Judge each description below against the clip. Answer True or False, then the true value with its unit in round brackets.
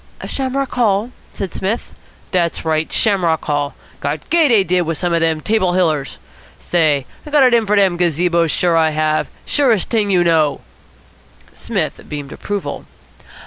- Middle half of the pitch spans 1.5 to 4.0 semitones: False (4.9 semitones)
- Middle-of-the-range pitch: True (175 Hz)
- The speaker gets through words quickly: False (160 wpm)